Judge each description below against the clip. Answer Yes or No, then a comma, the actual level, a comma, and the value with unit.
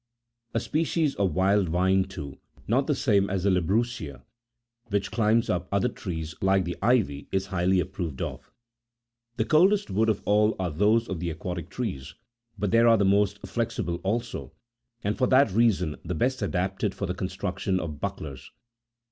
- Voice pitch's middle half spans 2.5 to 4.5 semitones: Yes, average, 4.0 semitones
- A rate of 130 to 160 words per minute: No, average, 170 wpm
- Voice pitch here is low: Yes, very low, 95 Hz